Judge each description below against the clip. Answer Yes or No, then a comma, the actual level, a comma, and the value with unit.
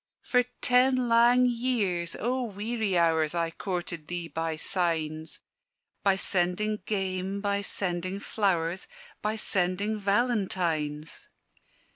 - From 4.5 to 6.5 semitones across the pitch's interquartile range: No, average, 4.1 semitones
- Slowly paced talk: Yes, slow, 105 wpm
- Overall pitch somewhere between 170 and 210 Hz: Yes, high, 190 Hz